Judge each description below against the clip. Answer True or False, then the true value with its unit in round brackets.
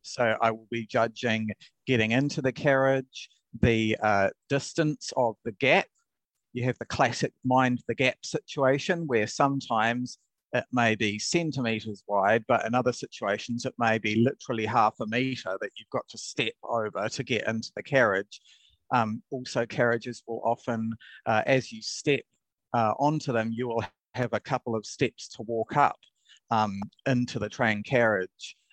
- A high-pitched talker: False (120 Hz)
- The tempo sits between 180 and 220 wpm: False (165 wpm)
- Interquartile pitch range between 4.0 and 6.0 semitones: False (2.8 semitones)